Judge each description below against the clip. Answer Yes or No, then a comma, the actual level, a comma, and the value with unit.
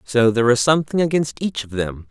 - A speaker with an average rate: No, fast, 230 wpm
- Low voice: Yes, low, 130 Hz